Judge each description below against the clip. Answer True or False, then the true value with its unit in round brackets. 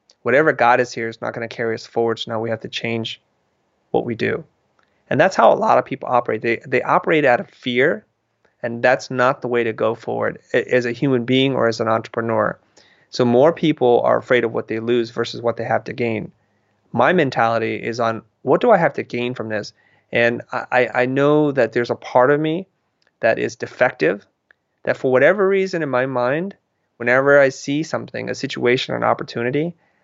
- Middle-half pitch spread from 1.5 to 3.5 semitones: True (3.1 semitones)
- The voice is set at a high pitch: False (120 Hz)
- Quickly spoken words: True (210 wpm)